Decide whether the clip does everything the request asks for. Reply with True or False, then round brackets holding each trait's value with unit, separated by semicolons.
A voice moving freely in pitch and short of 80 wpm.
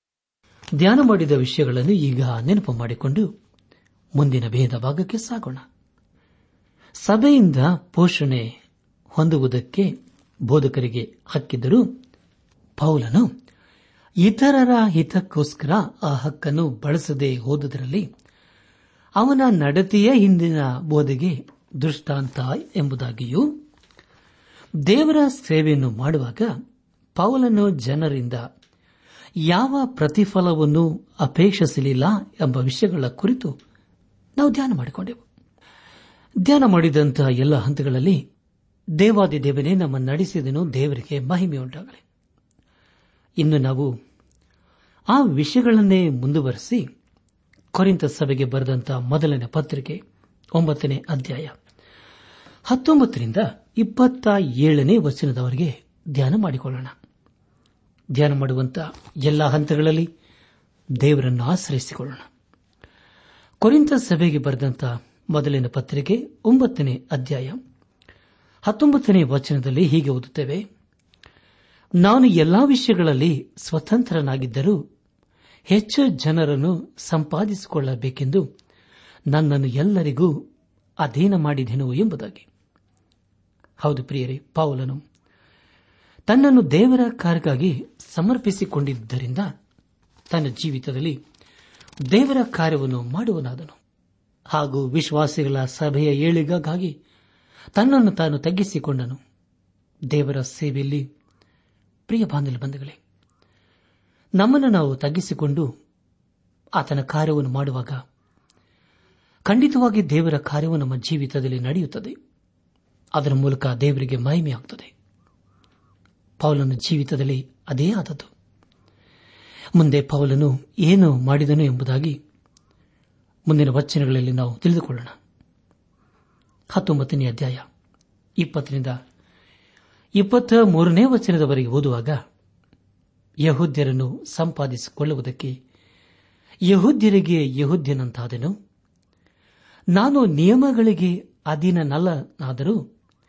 True (5.7 semitones; 65 wpm)